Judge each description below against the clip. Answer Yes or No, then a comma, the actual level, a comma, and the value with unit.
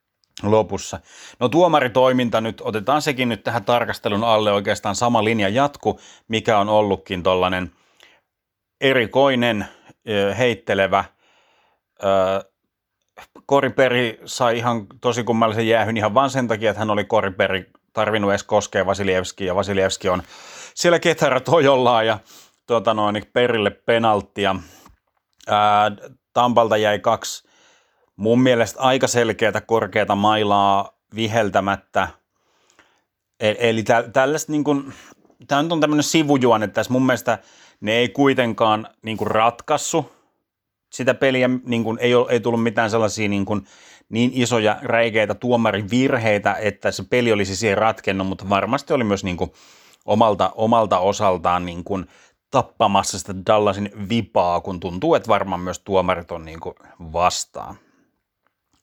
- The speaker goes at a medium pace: Yes, average, 120 wpm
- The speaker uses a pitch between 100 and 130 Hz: Yes, low, 110 Hz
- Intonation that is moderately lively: Yes, average, 3.5 semitones